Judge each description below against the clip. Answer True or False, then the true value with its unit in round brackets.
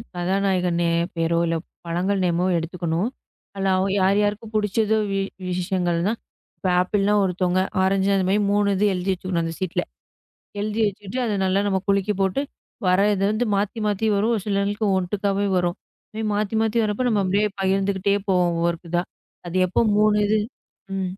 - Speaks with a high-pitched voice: True (195 Hz)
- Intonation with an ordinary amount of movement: False (2.3 semitones)